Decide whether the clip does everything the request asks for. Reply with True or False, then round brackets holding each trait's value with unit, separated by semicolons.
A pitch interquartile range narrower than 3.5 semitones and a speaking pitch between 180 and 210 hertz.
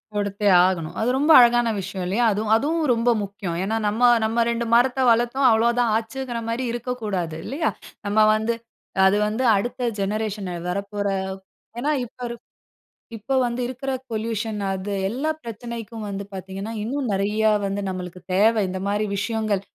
False (3.1 semitones; 220 Hz)